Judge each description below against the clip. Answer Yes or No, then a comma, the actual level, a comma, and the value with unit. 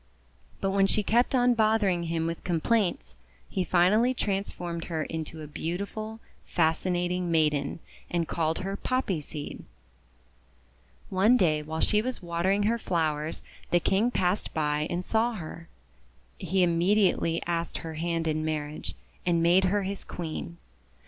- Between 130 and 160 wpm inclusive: Yes, average, 145 wpm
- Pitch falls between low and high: Yes, medium, 175 Hz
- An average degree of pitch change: Yes, average, 3.7 semitones